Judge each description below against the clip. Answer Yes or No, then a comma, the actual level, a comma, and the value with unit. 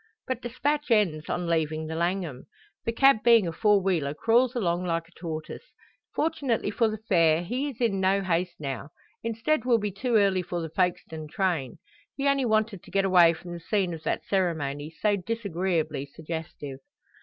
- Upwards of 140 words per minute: Yes, average, 180 wpm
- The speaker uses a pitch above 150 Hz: Yes, medium, 185 Hz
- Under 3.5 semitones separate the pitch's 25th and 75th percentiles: No, wide, 5.5 semitones